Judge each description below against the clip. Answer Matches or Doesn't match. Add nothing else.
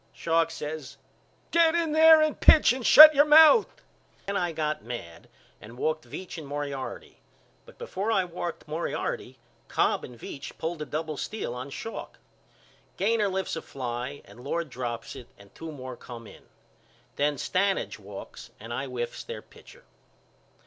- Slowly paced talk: Doesn't match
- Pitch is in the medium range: Matches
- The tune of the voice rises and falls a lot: Matches